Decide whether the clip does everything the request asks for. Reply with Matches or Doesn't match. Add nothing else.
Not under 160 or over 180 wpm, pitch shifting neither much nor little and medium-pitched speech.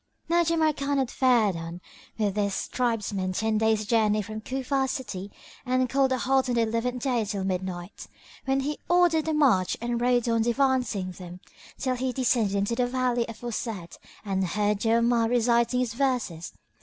Doesn't match